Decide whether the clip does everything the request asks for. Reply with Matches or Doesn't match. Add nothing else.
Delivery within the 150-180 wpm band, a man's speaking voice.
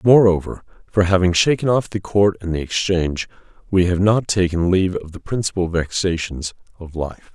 Matches